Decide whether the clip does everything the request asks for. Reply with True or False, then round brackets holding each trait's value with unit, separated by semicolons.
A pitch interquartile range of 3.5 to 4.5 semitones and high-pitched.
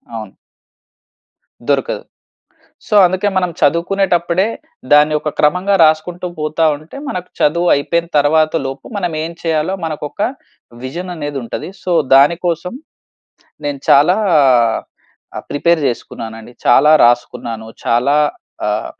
False (3.8 semitones; 155 Hz)